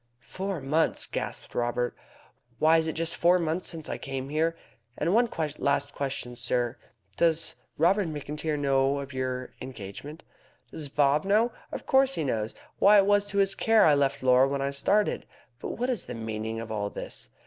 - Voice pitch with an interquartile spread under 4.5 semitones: No, average, 4.9 semitones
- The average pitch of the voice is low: No, medium, 145 Hz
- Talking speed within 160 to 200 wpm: Yes, average, 180 wpm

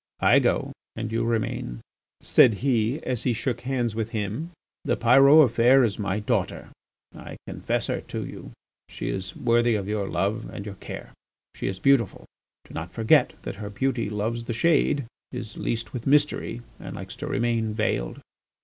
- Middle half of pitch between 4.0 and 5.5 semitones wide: No, average, 3.2 semitones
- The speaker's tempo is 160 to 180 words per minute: Yes, average, 175 wpm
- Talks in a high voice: No, low, 115 Hz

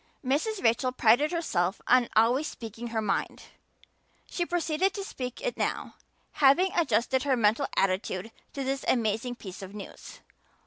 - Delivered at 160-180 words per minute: No, average, 145 wpm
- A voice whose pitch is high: Yes, very high, 250 Hz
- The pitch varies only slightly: No, average, 5.2 semitones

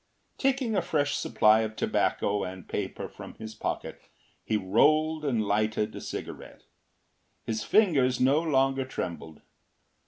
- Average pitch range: No, wide, 6.0 semitones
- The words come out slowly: Yes, slow, 130 wpm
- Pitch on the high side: No, low, 125 Hz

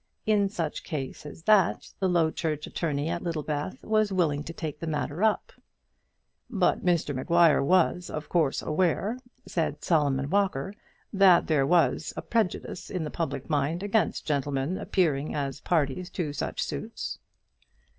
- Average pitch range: Yes, average, 3.9 semitones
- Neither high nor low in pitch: Yes, medium, 165 Hz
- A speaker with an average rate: Yes, average, 150 wpm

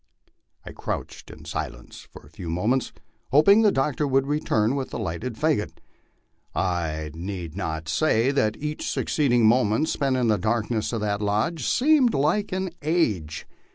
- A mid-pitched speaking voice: No, low, 120 Hz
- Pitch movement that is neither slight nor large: No, wide, 6.9 semitones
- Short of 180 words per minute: Yes, average, 160 wpm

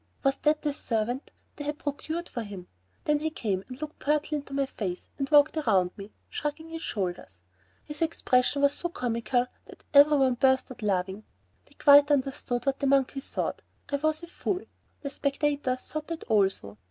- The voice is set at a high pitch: Yes, very high, 275 Hz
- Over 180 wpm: Yes, average, 190 wpm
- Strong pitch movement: No, average, 4.3 semitones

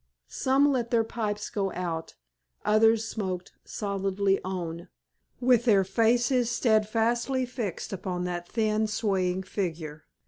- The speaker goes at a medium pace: No, slow, 115 wpm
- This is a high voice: Yes, high, 210 Hz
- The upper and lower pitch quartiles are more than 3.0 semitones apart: Yes, average, 3.9 semitones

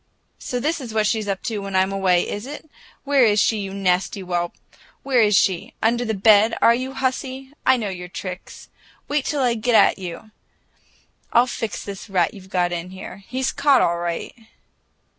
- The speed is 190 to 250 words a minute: Yes, average, 195 wpm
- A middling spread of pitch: Yes, average, 4.8 semitones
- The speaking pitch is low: No, high, 210 Hz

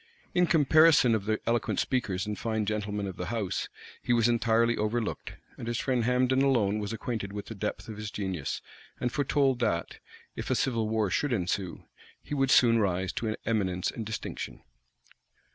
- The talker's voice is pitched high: No, low, 110 Hz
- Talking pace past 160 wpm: Yes, average, 180 wpm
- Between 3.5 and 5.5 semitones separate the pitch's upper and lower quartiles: No, average, 3.1 semitones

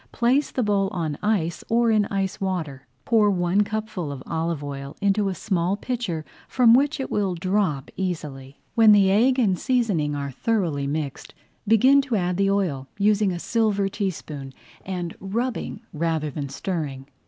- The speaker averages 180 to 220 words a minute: No, average, 165 wpm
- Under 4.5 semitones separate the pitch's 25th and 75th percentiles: No, wide, 5.5 semitones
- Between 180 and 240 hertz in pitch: Yes, high, 190 Hz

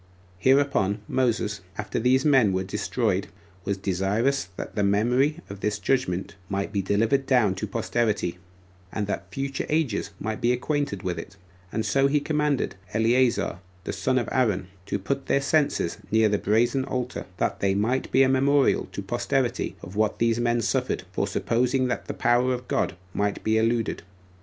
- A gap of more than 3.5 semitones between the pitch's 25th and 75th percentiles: Yes, average, 4.5 semitones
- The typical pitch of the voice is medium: No, low, 115 Hz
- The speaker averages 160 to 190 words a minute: Yes, average, 170 wpm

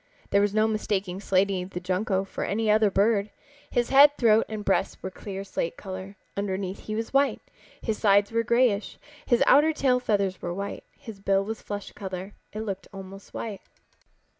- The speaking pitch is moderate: No, high, 205 Hz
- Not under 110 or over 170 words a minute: No, average, 180 wpm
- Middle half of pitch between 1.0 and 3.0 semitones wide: Yes, narrow, 2.4 semitones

